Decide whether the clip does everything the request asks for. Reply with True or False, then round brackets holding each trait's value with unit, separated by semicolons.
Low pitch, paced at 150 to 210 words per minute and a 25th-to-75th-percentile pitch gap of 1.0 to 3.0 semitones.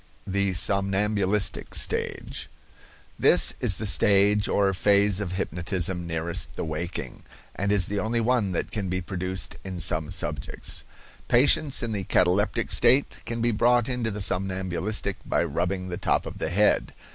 True (95 Hz; 155 wpm; 2.7 semitones)